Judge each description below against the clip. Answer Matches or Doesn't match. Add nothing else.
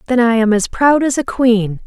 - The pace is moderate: Doesn't match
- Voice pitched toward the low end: Doesn't match